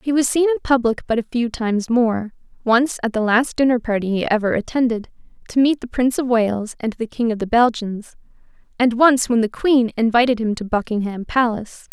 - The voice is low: No, high, 235 Hz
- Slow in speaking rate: No, average, 200 wpm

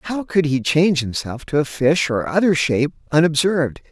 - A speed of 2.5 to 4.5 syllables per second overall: No, 5.5 syllables/s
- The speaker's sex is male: Yes, male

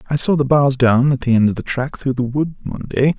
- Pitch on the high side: No, low, 135 Hz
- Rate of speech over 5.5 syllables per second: Yes, 5.9 syllables/s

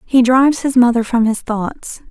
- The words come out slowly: No, average, 200 wpm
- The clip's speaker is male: No, female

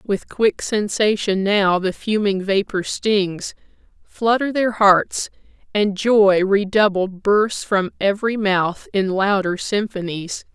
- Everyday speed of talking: No, slow, 120 wpm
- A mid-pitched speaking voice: No, high, 200 Hz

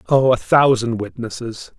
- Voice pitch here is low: Yes, low, 120 Hz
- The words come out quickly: No, slow, 135 wpm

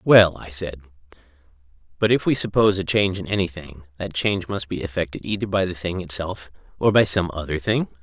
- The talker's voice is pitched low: Yes, very low, 90 Hz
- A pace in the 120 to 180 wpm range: No, average, 195 wpm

